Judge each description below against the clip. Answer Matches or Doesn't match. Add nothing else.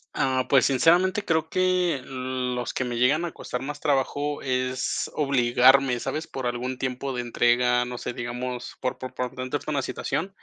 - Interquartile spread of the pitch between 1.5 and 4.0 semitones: Matches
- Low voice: Matches